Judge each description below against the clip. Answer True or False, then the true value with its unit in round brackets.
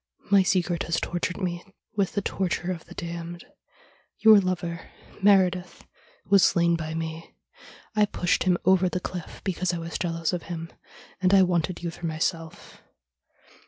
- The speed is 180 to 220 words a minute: False (160 wpm)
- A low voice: False (175 Hz)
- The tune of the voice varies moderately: False (1.8 semitones)